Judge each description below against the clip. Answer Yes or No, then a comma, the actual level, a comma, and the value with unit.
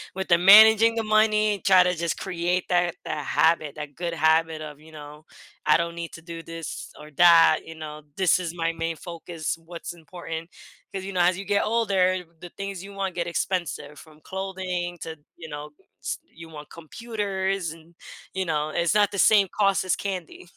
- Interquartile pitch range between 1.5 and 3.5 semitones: Yes, average, 2.9 semitones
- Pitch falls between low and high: Yes, medium, 175 Hz